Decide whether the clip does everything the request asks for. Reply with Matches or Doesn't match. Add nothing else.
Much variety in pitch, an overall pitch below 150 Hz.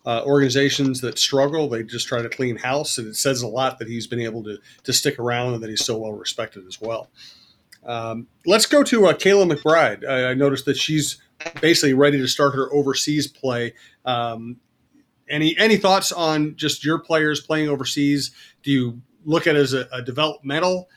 Doesn't match